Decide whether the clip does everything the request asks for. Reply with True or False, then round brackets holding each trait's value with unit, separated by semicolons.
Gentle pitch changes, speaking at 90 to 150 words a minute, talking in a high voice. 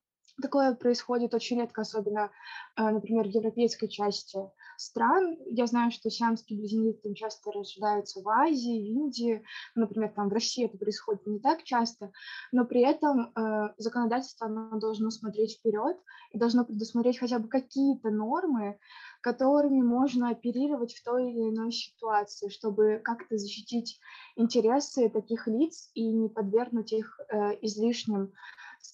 True (2.3 semitones; 135 wpm; 230 Hz)